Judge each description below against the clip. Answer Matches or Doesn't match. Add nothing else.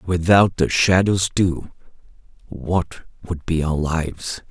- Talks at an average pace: Doesn't match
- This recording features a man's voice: Matches